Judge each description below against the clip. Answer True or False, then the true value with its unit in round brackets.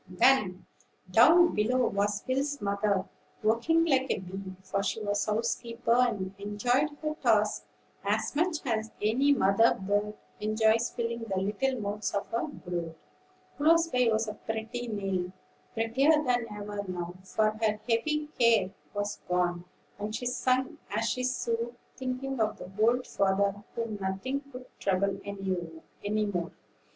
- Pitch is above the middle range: True (220 Hz)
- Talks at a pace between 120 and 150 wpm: True (140 wpm)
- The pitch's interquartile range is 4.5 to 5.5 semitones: False (3.9 semitones)